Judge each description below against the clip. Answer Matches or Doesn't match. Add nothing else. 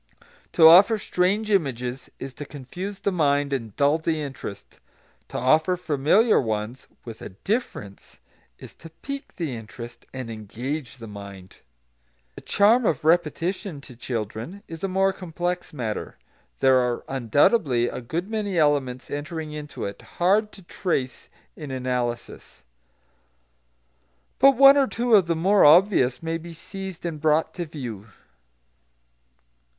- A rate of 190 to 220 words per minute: Doesn't match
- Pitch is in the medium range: Matches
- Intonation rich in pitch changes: Matches